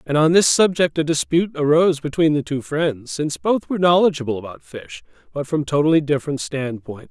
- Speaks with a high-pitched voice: No, medium, 155 Hz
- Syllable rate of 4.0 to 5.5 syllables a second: No, 5.9 syllables/s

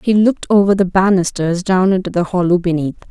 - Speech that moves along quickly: No, average, 195 wpm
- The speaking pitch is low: No, medium, 185 Hz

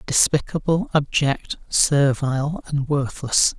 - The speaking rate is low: Yes, slow, 85 wpm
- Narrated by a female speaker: No, male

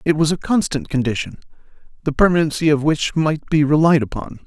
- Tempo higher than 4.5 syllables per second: Yes, 5.8 syllables/s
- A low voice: No, medium, 155 Hz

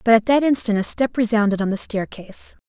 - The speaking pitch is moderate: No, high, 220 Hz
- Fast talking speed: Yes, fast, 225 wpm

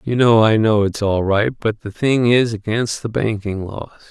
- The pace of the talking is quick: Yes, fast, 220 wpm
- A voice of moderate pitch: No, low, 110 Hz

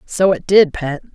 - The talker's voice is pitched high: No, medium, 175 Hz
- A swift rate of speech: Yes, fast, 210 wpm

